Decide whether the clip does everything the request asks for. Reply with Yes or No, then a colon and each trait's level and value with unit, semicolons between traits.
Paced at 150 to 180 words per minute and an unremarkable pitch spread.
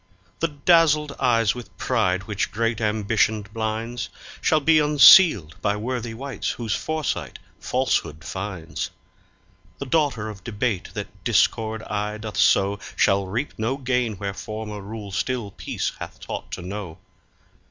No: average, 140 wpm; average, 3.8 semitones